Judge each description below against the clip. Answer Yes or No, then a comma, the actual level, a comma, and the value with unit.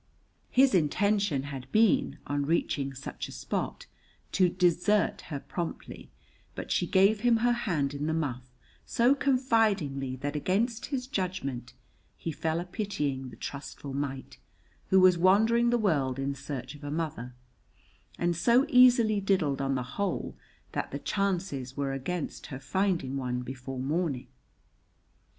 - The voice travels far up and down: Yes, wide, 6.9 semitones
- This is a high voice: No, medium, 165 Hz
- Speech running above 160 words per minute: No, average, 145 wpm